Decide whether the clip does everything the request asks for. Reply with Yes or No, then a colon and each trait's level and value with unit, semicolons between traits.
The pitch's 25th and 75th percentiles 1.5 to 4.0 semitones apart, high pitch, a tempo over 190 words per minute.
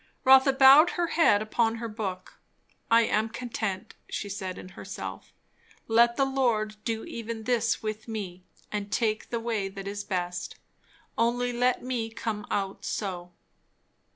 No: average, 2.8 semitones; high, 225 Hz; average, 150 wpm